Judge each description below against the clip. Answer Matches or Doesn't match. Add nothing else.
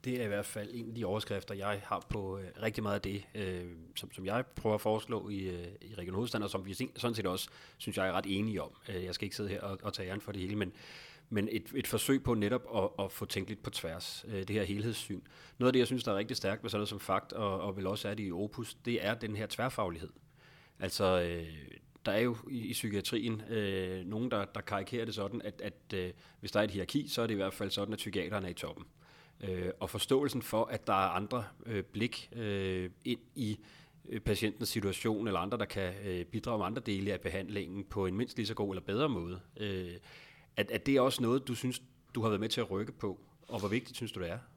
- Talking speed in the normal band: Doesn't match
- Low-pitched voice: Matches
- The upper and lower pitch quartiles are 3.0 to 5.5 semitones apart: Matches